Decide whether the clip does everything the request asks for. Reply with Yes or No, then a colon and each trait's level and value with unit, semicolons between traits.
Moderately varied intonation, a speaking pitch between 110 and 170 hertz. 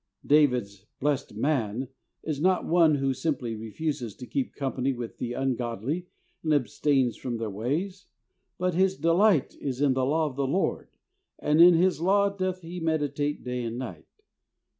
Yes: average, 5.0 semitones; medium, 140 Hz